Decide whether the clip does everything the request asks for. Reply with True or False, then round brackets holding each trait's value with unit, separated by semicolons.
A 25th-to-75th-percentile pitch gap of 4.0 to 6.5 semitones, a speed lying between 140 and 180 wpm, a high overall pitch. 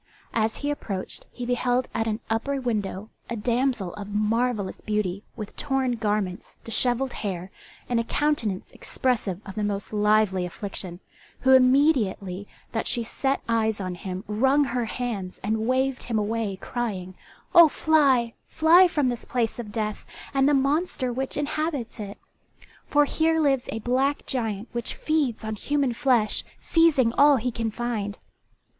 True (4.3 semitones; 155 wpm; 235 Hz)